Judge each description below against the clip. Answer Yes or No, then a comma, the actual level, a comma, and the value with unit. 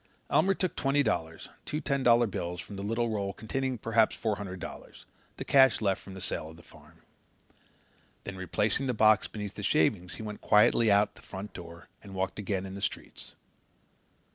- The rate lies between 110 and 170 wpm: No, average, 195 wpm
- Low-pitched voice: Yes, low, 105 Hz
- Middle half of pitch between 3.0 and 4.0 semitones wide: Yes, average, 3.4 semitones